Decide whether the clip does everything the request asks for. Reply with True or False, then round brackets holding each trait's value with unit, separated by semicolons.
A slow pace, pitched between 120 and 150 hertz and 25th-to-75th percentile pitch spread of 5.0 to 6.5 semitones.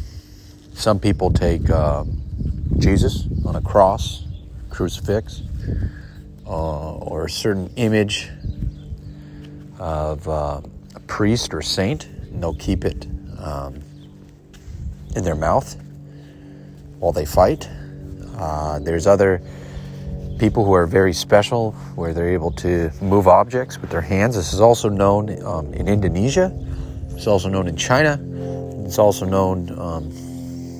False (125 wpm; 90 Hz; 5.4 semitones)